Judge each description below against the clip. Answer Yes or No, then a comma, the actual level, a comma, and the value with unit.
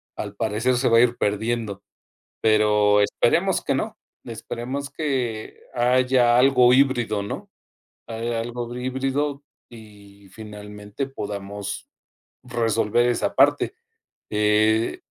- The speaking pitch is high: No, low, 115 Hz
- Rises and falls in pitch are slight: No, average, 3.2 semitones